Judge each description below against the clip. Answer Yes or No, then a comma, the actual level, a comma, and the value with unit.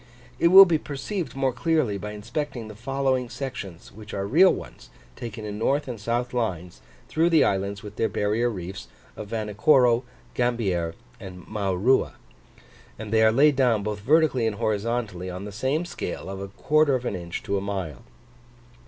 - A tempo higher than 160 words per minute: Yes, average, 175 wpm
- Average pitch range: Yes, average, 4.9 semitones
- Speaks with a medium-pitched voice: No, low, 110 Hz